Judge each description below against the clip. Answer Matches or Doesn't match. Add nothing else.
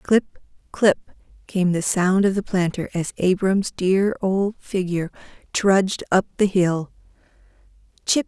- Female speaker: Matches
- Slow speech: Matches